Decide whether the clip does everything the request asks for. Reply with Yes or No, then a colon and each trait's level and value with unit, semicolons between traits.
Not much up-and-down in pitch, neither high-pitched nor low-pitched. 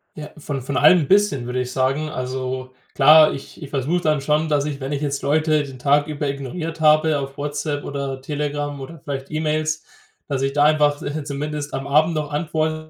Yes: narrow, 2.0 semitones; medium, 145 Hz